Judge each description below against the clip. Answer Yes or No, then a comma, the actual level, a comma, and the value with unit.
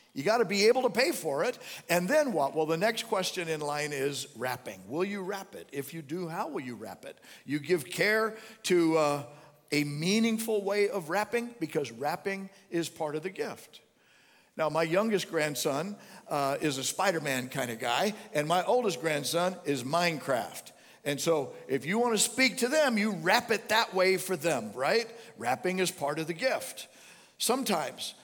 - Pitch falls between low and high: Yes, medium, 175 Hz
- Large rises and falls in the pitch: Yes, wide, 6.3 semitones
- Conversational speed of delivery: Yes, average, 190 wpm